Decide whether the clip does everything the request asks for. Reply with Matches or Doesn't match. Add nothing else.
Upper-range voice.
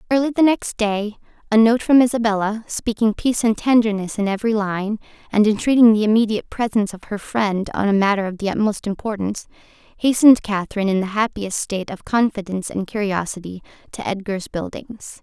Matches